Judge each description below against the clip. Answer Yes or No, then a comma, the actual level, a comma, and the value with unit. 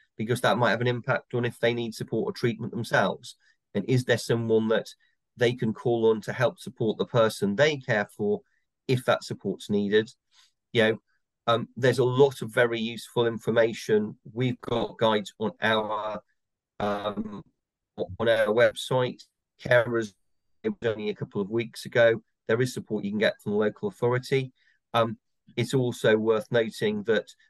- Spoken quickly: No, average, 170 wpm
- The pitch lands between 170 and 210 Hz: No, low, 120 Hz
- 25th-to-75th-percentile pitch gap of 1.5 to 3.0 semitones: Yes, average, 2.7 semitones